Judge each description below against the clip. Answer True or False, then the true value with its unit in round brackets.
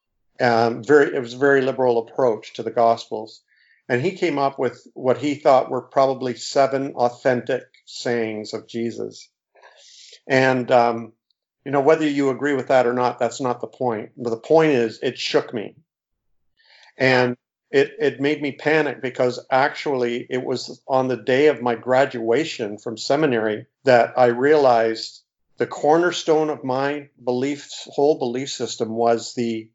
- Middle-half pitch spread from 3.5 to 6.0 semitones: False (3.1 semitones)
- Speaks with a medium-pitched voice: False (125 Hz)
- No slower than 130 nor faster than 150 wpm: False (160 wpm)